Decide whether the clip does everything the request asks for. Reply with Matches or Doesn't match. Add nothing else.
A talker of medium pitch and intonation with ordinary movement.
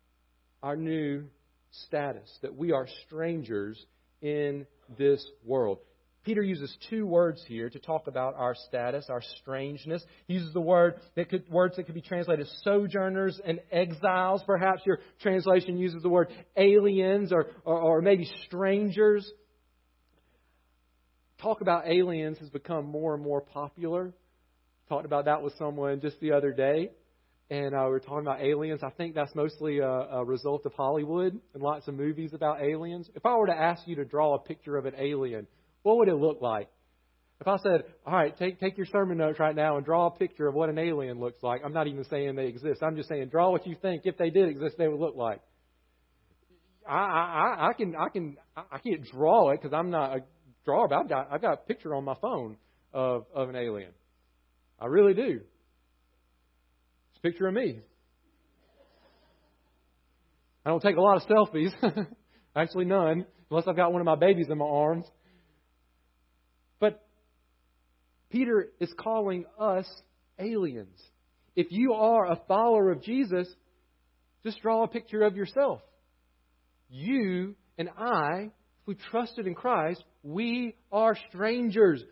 Doesn't match